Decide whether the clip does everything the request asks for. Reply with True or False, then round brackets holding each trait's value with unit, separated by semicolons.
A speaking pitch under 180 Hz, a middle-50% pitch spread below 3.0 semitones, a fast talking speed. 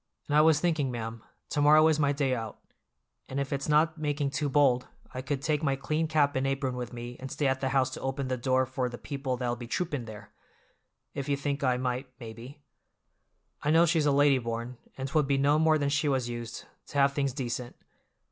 True (135 Hz; 2.6 semitones; 225 wpm)